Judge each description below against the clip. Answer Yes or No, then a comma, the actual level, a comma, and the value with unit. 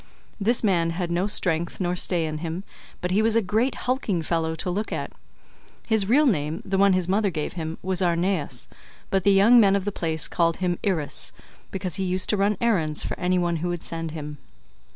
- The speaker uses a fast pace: Yes, fast, 215 wpm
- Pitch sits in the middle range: Yes, medium, 180 Hz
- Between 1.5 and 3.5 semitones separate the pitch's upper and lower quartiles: Yes, average, 3.2 semitones